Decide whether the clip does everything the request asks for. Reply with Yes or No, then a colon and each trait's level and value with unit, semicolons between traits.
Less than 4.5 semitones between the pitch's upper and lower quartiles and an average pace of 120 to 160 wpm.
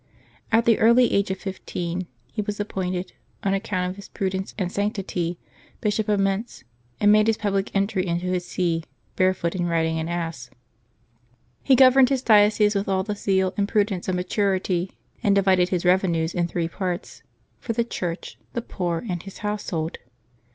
No: average, 2.7 semitones; average, 175 wpm